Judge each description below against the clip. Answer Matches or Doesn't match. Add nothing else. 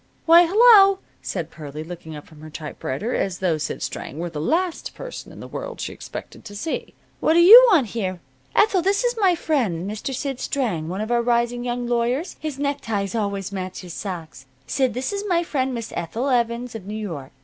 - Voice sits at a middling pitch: Doesn't match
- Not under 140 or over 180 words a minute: Doesn't match